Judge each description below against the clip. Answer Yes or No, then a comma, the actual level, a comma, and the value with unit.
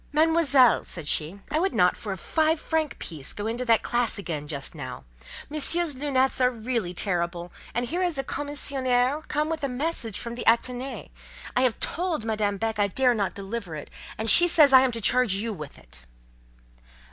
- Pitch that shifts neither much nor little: No, wide, 6.3 semitones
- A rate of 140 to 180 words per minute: No, average, 195 wpm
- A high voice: Yes, high, 245 Hz